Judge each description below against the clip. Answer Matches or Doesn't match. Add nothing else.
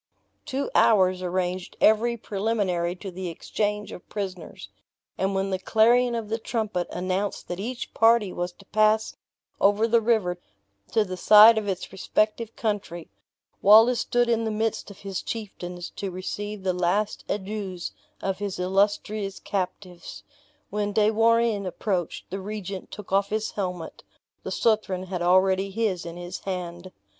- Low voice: Doesn't match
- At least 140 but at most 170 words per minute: Matches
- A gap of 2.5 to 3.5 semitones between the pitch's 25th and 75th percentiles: Matches